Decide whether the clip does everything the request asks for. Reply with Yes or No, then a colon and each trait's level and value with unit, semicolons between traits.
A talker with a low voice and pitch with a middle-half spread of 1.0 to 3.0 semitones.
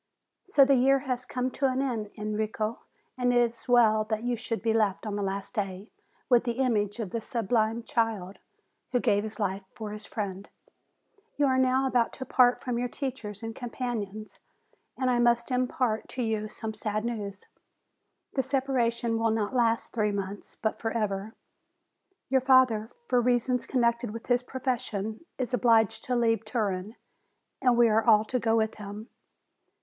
No: high, 230 Hz; narrow, 2.6 semitones